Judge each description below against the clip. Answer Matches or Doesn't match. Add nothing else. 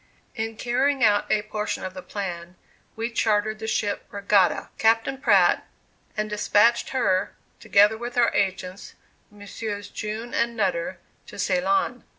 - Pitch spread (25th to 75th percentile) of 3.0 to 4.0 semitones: Doesn't match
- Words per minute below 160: Matches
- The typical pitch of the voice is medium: Doesn't match